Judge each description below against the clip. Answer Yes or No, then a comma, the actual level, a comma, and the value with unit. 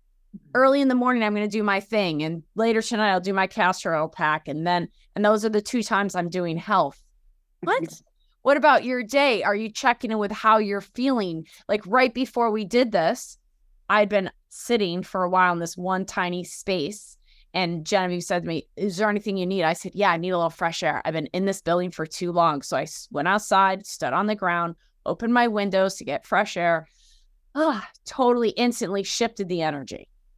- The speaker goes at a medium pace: No, fast, 215 wpm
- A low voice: No, high, 195 Hz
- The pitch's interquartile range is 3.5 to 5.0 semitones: Yes, average, 3.9 semitones